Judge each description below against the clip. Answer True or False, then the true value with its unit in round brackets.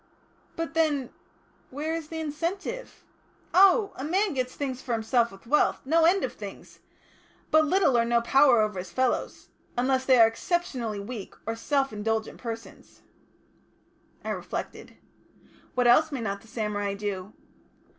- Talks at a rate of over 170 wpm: False (155 wpm)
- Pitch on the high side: True (255 Hz)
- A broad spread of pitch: True (5.8 semitones)